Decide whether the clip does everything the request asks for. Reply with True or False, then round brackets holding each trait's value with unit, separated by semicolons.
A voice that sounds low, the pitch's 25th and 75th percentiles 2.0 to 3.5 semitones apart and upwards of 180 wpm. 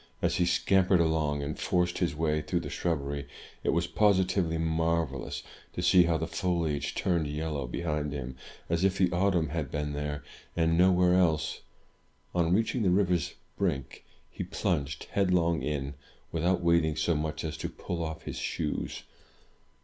False (80 Hz; 2.9 semitones; 165 wpm)